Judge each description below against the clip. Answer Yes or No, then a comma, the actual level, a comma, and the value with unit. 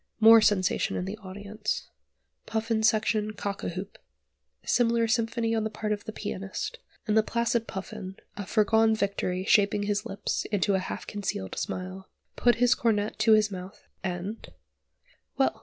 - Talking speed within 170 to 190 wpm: No, average, 155 wpm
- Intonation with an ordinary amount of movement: No, narrow, 2.2 semitones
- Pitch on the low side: No, high, 210 Hz